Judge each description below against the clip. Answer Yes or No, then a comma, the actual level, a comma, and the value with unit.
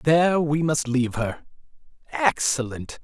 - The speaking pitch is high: No, medium, 145 Hz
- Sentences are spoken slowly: Yes, slow, 120 wpm